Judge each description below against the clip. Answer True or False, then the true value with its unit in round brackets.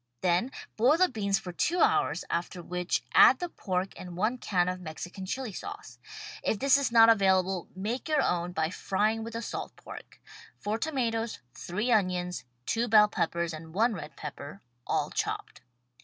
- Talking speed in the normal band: True (170 wpm)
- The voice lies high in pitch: True (200 Hz)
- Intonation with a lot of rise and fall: False (4.4 semitones)